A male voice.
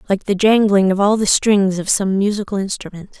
No: female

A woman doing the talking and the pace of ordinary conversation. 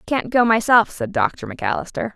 Yes: female; average, 165 wpm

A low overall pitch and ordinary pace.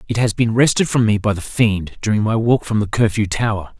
No: low, 110 Hz; fast, 255 wpm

